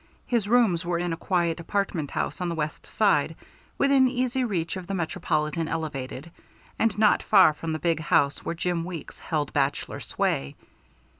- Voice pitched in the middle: Yes, medium, 170 Hz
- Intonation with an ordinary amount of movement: Yes, average, 4.0 semitones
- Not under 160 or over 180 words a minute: Yes, average, 170 wpm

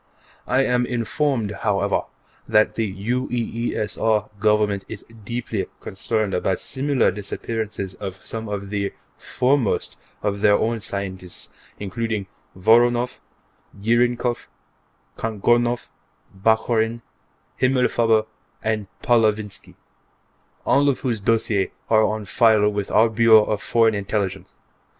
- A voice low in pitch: Yes, low, 110 Hz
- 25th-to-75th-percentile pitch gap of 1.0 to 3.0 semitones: Yes, average, 2.7 semitones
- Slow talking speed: Yes, slow, 105 wpm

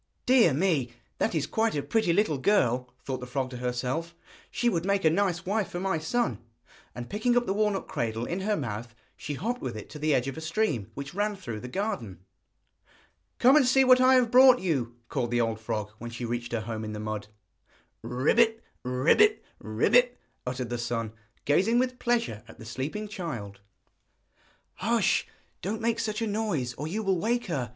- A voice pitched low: No, medium, 160 Hz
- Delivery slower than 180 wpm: No, average, 195 wpm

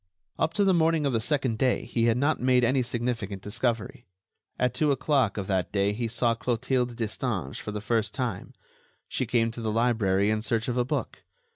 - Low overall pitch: Yes, low, 120 Hz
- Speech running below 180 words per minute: No, fast, 205 wpm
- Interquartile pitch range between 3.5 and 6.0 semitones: No, average, 2.9 semitones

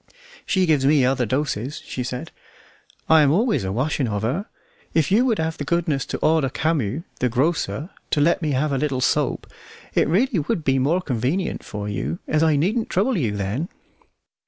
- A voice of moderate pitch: Yes, medium, 150 Hz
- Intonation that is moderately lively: Yes, average, 4.8 semitones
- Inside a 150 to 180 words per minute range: No, average, 190 wpm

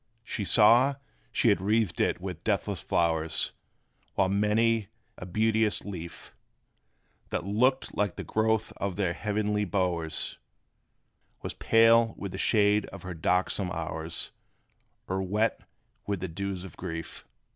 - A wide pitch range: No, average, 3.2 semitones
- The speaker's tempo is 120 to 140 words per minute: Yes, slow, 135 wpm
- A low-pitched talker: Yes, low, 100 Hz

